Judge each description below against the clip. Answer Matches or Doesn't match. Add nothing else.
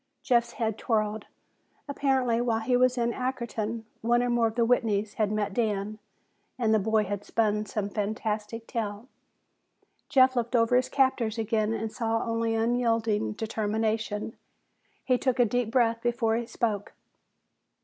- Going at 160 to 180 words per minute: Doesn't match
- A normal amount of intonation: Doesn't match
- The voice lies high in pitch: Matches